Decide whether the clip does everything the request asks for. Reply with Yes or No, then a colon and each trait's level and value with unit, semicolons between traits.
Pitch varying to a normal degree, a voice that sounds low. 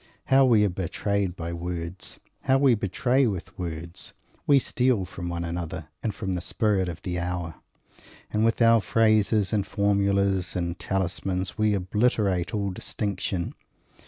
Yes: average, 3.4 semitones; very low, 95 Hz